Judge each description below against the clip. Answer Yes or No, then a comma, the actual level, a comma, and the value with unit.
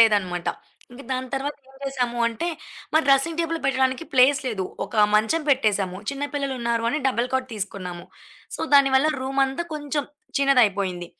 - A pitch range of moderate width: Yes, average, 4.5 semitones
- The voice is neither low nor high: No, very high, 260 Hz